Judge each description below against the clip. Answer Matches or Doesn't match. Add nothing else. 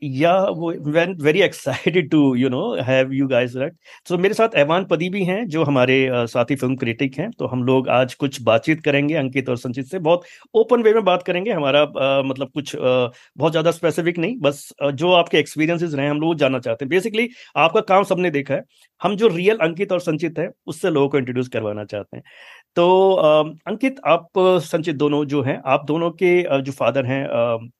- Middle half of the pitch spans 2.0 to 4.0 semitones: Doesn't match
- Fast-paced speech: Matches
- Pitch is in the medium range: Matches